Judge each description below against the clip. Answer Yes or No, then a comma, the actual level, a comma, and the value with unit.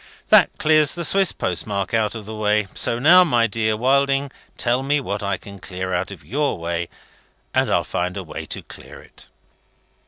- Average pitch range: No, wide, 6.1 semitones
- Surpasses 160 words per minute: Yes, average, 190 wpm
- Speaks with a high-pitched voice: No, low, 110 Hz